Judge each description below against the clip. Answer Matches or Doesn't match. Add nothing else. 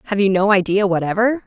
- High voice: Matches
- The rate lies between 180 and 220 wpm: Matches